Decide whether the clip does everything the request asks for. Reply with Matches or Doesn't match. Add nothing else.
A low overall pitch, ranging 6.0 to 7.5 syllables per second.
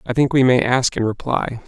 Doesn't match